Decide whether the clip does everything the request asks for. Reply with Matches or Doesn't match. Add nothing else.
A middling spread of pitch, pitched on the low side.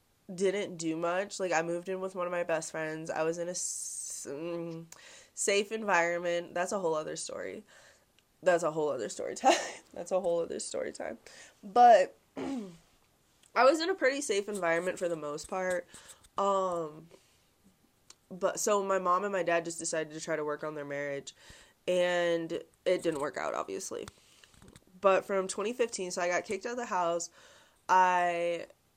Doesn't match